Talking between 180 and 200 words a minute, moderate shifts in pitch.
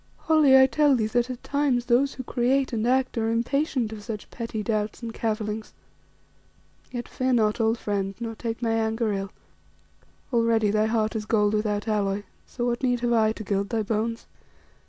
No: average, 185 wpm; narrow, 2.3 semitones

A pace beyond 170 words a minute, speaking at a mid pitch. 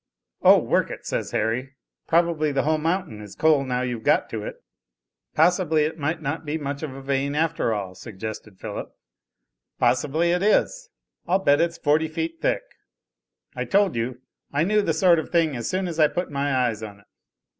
Yes: average, 190 wpm; medium, 150 Hz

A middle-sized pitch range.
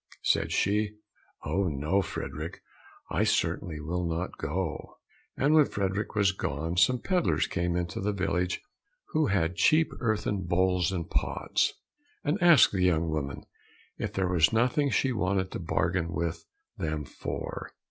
Yes: average, 3.9 semitones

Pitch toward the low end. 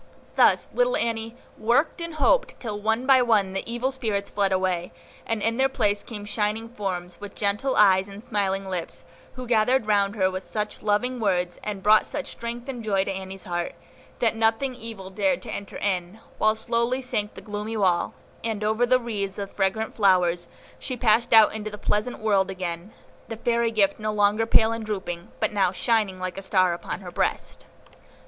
No: high, 210 Hz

